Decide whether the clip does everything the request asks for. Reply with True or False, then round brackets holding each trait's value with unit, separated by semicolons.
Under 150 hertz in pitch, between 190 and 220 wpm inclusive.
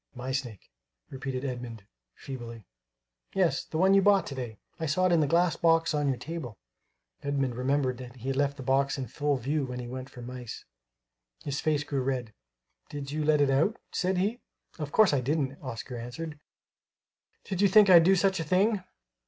True (140 Hz; 195 wpm)